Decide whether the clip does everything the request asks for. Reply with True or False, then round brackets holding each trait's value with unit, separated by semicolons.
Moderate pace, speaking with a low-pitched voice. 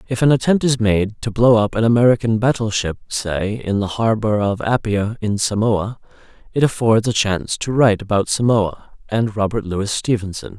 True (175 wpm; 110 Hz)